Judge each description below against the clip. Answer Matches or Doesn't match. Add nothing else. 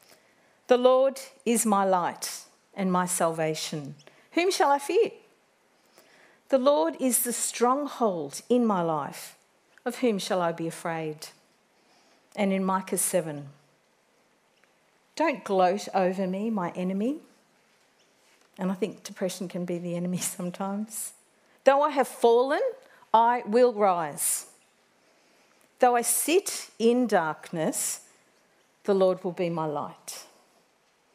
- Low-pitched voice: Doesn't match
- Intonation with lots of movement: Matches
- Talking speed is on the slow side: Matches